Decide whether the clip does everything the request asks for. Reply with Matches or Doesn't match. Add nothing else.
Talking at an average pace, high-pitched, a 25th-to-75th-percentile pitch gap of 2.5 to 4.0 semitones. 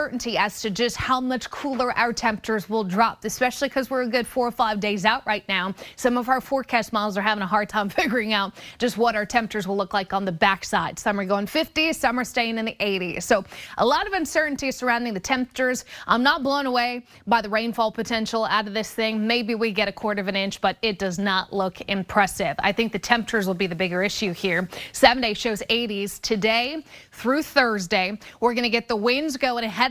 Doesn't match